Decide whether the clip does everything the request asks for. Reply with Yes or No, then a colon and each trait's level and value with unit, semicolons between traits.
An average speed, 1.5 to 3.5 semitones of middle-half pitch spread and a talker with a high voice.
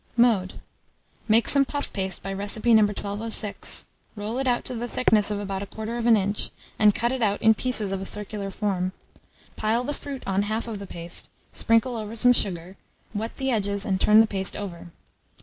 Yes: average, 190 wpm; average, 2.8 semitones; high, 210 Hz